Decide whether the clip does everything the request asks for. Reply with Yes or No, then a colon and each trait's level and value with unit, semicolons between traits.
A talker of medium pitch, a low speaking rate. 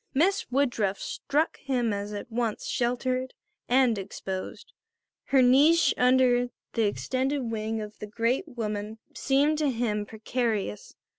No: high, 245 Hz; slow, 130 wpm